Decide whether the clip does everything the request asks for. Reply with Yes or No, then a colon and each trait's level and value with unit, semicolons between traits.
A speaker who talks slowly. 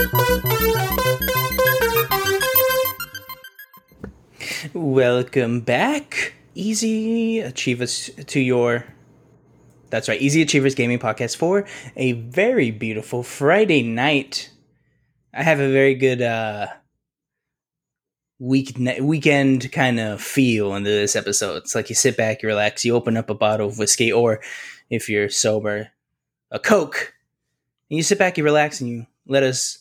Yes: slow, 125 wpm